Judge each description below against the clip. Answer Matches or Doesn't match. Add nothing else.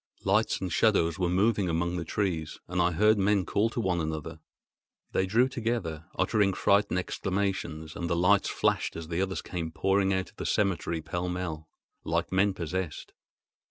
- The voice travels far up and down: Doesn't match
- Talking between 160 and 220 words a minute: Matches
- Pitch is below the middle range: Matches